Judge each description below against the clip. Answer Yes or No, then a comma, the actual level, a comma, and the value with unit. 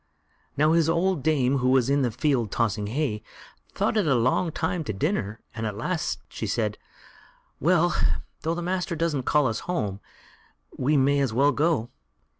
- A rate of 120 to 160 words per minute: No, average, 175 wpm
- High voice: No, medium, 140 Hz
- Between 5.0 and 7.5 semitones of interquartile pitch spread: Yes, wide, 5.6 semitones